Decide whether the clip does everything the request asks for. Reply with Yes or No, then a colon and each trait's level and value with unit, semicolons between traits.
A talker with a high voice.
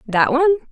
Yes: very high, 270 Hz